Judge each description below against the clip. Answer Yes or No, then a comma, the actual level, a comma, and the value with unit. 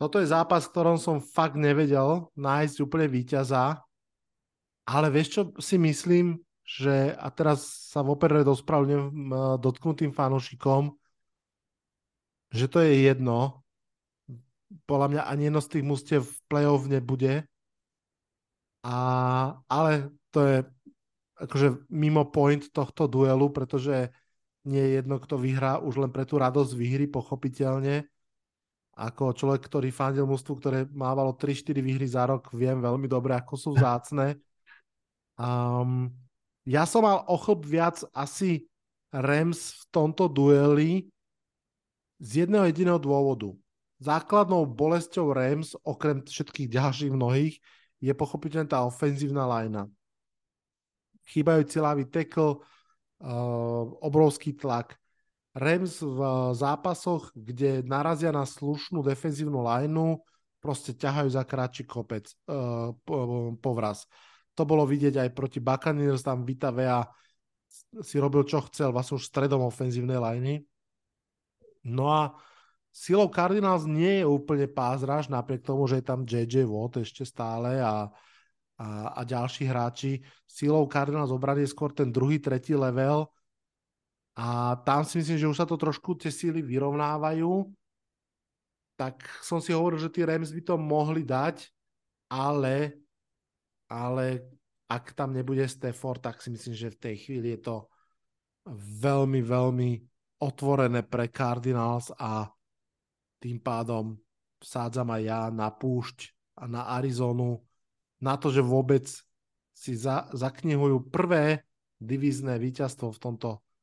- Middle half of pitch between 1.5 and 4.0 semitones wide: Yes, average, 3.1 semitones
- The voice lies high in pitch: No, low, 135 Hz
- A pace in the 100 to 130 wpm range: Yes, average, 125 wpm